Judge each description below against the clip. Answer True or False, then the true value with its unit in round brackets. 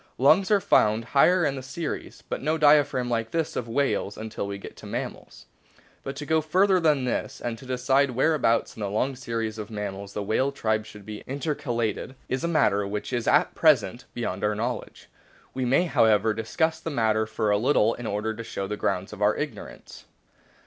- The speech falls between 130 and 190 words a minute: False (205 wpm)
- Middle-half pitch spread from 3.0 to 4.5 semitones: False (4.9 semitones)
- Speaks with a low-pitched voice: True (120 Hz)